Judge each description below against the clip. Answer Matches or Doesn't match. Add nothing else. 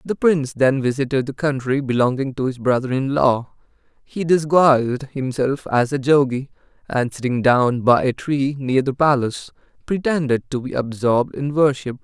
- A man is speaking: Matches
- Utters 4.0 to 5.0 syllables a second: Matches